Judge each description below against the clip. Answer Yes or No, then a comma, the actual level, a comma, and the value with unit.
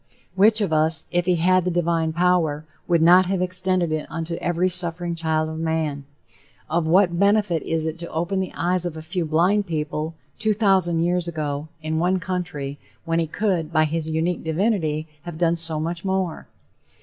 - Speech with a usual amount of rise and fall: No, narrow, 2.3 semitones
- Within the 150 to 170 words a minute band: No, average, 185 wpm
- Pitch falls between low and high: Yes, medium, 170 Hz